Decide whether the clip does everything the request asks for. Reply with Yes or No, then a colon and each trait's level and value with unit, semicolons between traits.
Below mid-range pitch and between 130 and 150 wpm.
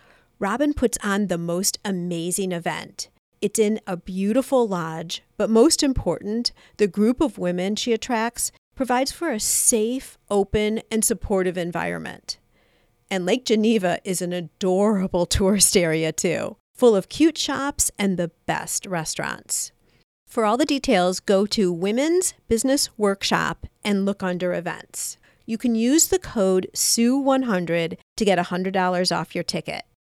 No: high, 205 Hz; average, 140 wpm